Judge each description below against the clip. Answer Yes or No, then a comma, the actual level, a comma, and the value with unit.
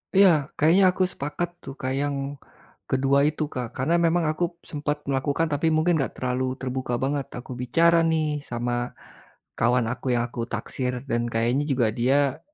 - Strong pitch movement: No, average, 3.7 semitones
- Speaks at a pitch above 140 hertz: No, low, 135 Hz